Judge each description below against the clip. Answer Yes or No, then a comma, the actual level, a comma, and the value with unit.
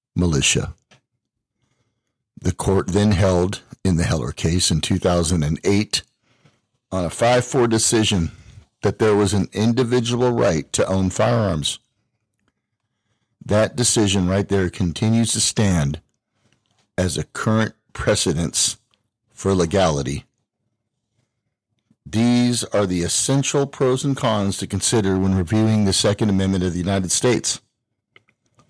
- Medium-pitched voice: No, low, 110 Hz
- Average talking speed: No, slow, 115 wpm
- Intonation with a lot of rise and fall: No, average, 3.7 semitones